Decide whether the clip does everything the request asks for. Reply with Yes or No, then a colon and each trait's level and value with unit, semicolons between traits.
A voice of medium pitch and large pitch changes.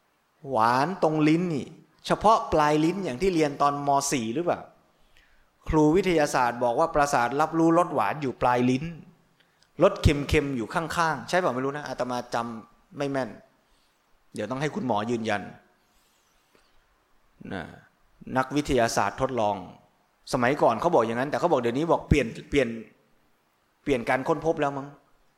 No: medium, 145 Hz; average, 4.4 semitones